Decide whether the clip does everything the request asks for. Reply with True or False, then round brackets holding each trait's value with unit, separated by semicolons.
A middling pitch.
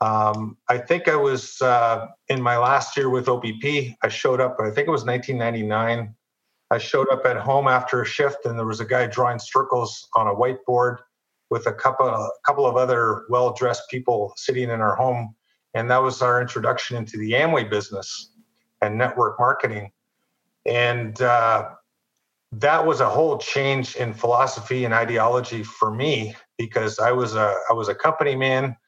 False (125 Hz)